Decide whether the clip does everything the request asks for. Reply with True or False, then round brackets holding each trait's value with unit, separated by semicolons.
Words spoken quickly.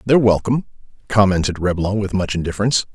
False (145 wpm)